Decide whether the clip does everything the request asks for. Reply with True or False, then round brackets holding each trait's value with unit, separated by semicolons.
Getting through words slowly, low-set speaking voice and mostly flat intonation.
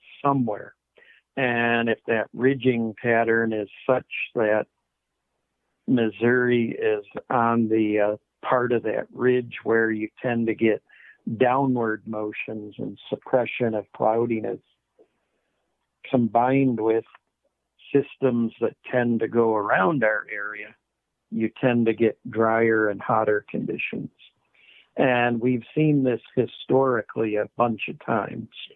True (115 wpm; 115 Hz; 2.0 semitones)